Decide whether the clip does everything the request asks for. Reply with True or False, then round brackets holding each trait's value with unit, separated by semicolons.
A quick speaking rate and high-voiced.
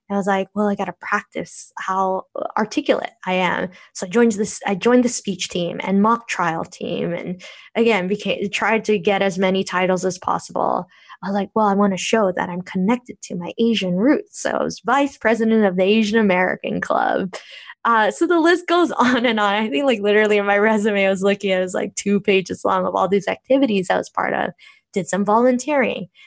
True (220 wpm; 205 Hz)